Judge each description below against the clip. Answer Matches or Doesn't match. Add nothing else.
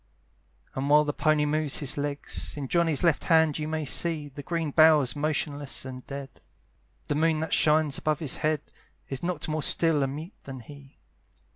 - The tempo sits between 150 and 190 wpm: Matches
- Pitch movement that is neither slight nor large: Doesn't match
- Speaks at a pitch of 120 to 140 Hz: Doesn't match